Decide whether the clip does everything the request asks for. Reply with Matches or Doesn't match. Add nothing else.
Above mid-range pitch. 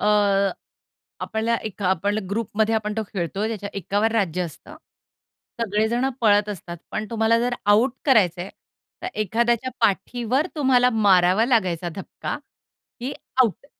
Matches